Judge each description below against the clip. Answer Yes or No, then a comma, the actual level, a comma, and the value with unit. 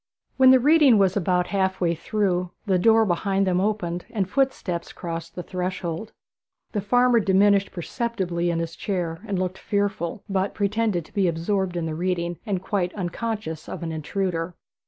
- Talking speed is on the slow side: No, average, 170 wpm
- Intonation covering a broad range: No, average, 3.1 semitones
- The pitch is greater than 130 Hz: Yes, high, 190 Hz